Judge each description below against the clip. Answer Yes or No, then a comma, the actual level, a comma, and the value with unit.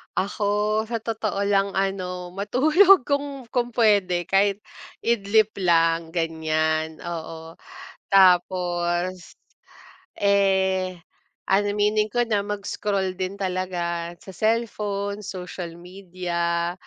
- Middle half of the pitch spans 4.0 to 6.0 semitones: No, average, 3.0 semitones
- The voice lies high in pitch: Yes, high, 195 Hz